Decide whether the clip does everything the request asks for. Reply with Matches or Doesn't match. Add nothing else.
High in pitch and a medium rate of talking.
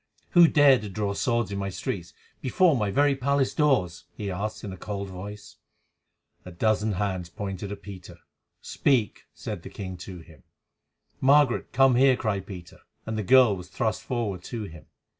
Doesn't match